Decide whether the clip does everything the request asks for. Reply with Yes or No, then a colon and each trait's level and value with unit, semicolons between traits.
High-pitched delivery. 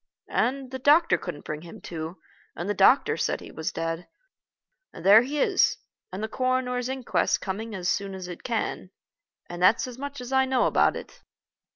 Yes: high, 220 Hz